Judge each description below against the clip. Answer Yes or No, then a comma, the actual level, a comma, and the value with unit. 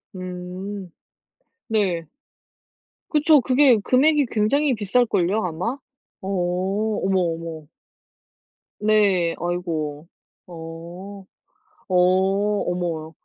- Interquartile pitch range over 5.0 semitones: No, average, 4.4 semitones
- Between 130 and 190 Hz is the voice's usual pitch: Yes, medium, 185 Hz